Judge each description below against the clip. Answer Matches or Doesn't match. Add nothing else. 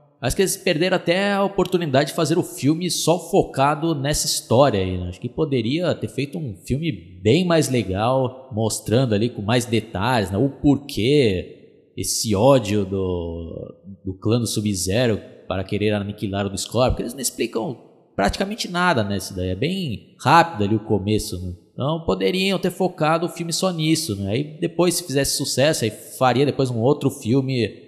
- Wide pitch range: Matches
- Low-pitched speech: Matches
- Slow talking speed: Doesn't match